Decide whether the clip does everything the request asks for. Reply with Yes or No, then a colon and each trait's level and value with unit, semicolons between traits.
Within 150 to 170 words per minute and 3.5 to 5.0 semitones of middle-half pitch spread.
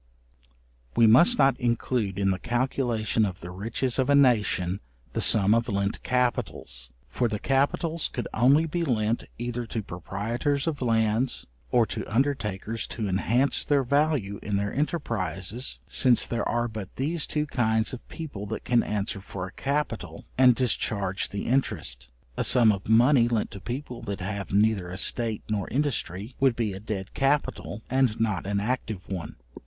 Yes: average, 165 wpm; average, 4.4 semitones